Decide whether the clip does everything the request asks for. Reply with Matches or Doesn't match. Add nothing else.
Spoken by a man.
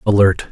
Matches